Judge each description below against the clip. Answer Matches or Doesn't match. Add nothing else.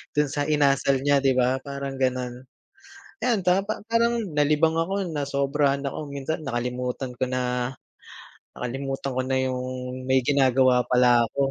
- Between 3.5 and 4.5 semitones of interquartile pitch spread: Doesn't match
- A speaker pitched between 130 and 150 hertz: Matches